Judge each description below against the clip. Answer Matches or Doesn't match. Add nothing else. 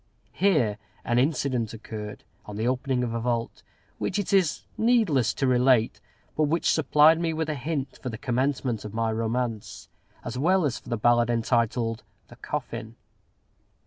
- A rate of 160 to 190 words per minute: Matches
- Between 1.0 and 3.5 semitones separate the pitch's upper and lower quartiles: Doesn't match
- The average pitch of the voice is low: Matches